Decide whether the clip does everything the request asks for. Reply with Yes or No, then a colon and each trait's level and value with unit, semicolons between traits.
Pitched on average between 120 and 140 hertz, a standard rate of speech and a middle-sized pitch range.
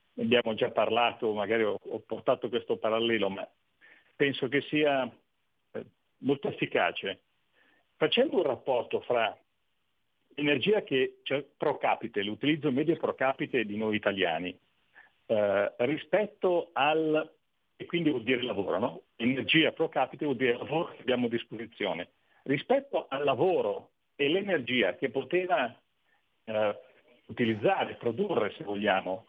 No: low, 135 Hz; average, 125 wpm; wide, 5.7 semitones